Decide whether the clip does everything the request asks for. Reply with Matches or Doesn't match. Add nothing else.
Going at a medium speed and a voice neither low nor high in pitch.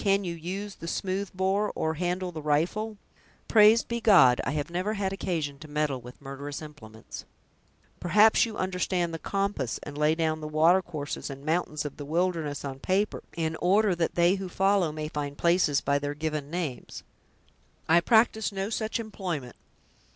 Matches